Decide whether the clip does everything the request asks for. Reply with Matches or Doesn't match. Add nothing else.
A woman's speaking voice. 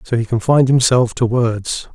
Doesn't match